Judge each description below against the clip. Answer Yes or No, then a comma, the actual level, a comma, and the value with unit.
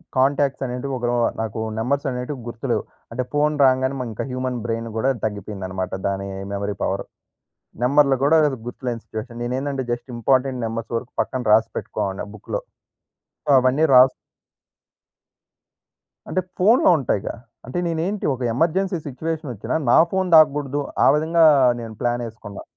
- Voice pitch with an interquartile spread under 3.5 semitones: No, average, 3.8 semitones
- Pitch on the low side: Yes, low, 130 Hz